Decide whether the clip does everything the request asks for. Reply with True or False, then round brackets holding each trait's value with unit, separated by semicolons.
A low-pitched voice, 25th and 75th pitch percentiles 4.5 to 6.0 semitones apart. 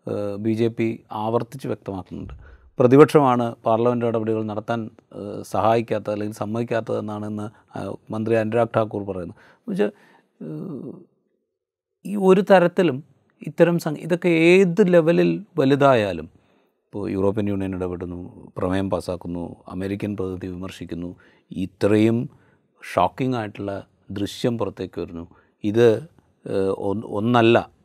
True (110 Hz; 4.8 semitones)